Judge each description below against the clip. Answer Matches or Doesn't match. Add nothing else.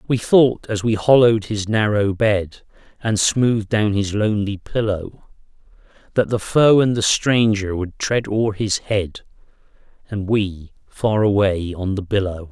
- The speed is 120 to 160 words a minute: Matches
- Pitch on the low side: Matches